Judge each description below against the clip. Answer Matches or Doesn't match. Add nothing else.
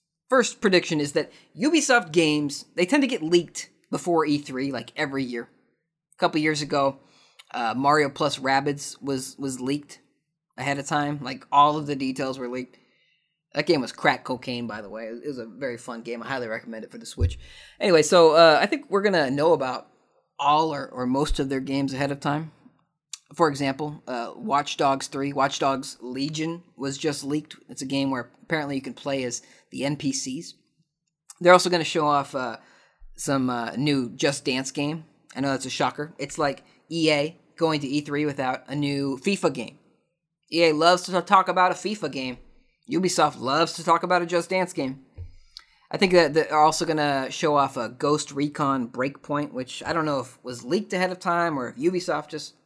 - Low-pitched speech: Doesn't match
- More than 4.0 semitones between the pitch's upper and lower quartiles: Doesn't match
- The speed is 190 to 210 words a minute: Matches